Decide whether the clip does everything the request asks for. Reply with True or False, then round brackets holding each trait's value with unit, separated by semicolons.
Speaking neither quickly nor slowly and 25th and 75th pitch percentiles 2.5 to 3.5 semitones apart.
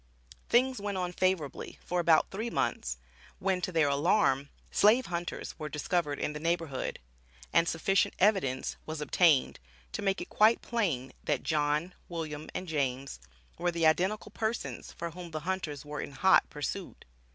False (160 wpm; 4.2 semitones)